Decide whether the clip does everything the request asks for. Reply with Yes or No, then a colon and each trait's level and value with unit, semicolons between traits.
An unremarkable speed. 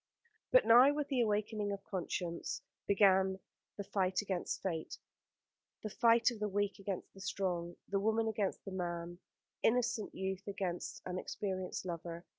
Yes: average, 150 wpm